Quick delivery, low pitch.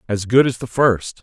Yes: fast, 245 wpm; low, 115 Hz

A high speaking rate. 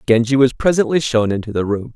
Yes: fast, 215 wpm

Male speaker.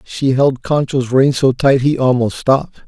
Yes: male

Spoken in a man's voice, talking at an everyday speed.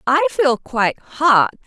No: female; average, 145 wpm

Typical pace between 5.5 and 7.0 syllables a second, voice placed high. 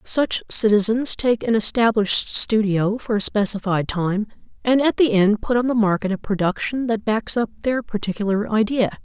No: 4.9 syllables/s; high, 215 Hz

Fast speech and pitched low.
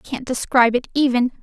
No: fast, 210 wpm; very high, 250 Hz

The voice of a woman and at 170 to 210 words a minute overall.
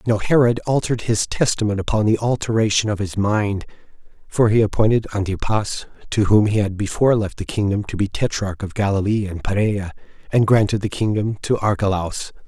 No: male; average, 180 wpm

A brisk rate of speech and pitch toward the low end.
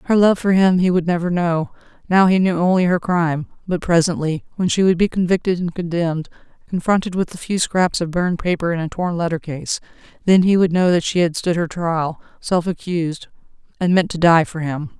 No: fast, 215 wpm; medium, 175 Hz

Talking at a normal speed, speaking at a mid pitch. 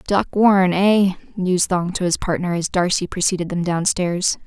Yes: average, 175 wpm; medium, 180 Hz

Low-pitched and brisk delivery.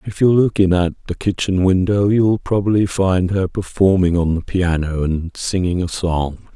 No: very low, 95 Hz; average, 185 wpm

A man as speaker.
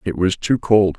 Yes: male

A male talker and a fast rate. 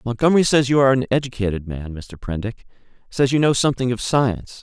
No: male; average, 195 wpm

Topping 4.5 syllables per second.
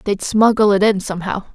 Yes: 5.8 syllables/s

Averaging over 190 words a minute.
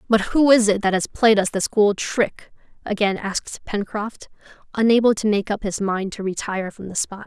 Yes: fast, 205 wpm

